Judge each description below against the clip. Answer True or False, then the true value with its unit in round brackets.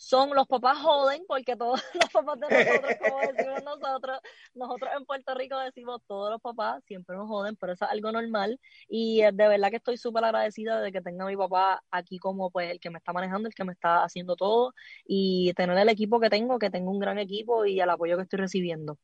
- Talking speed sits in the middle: False (230 wpm)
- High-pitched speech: True (210 Hz)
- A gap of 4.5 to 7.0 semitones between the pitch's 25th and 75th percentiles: True (5.0 semitones)